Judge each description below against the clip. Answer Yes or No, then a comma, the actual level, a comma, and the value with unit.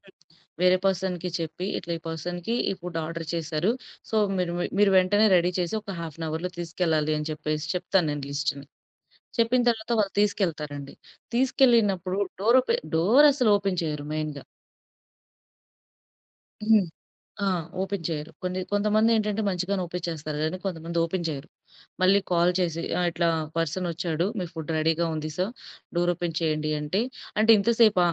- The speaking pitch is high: No, medium, 175 Hz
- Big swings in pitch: No, average, 3.6 semitones